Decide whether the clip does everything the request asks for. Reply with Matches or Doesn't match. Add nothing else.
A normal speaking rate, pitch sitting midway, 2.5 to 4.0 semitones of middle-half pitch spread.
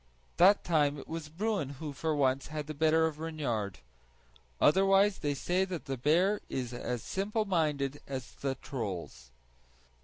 Doesn't match